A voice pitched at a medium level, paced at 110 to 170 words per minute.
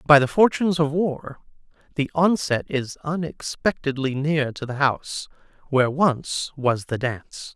Yes: medium, 145 Hz; average, 145 wpm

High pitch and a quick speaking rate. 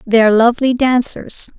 No: high, 235 Hz; slow, 115 wpm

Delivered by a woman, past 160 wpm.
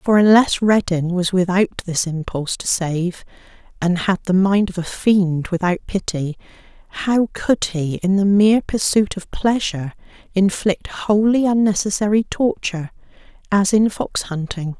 No: female; average, 140 wpm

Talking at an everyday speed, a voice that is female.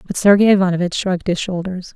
Yes: average, 185 wpm; female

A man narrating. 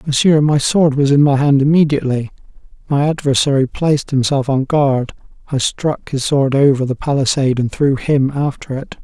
Yes: male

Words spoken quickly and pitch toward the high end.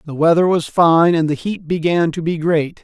No: fast, 235 wpm; medium, 165 Hz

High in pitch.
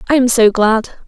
Yes: high, 245 Hz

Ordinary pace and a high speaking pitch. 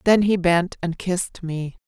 No: average, 190 wpm; medium, 180 Hz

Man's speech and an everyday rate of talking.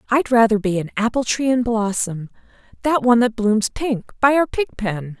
No: female; average, 185 wpm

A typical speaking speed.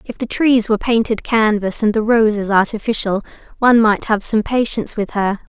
Yes: average, 185 wpm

